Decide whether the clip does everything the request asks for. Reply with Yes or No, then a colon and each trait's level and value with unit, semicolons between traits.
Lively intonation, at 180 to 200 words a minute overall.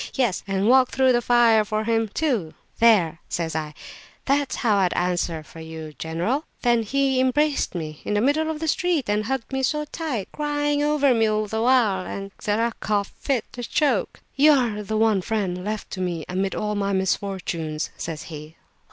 Yes: wide, 6.1 semitones; average, 190 wpm